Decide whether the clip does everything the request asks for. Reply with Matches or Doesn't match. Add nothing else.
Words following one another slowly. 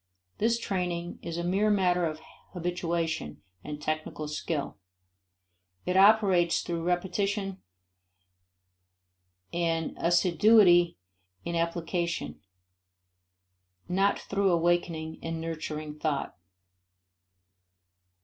Matches